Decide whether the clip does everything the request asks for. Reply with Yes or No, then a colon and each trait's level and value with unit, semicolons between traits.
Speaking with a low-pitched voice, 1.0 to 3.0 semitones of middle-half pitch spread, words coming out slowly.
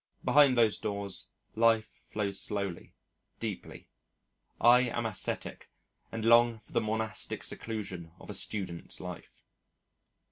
Yes: low, 110 Hz; narrow, 2.4 semitones; slow, 115 wpm